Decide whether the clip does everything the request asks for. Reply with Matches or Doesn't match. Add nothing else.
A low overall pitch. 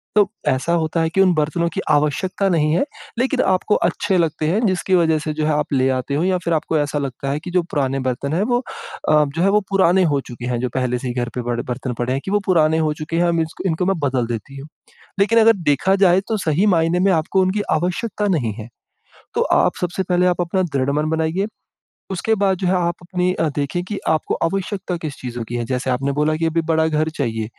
Doesn't match